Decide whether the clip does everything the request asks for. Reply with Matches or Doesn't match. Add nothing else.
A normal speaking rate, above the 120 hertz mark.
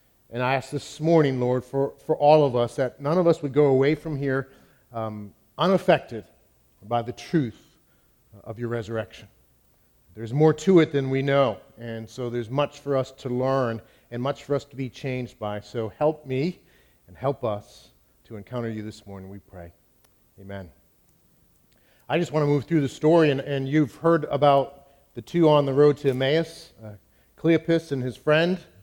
Matches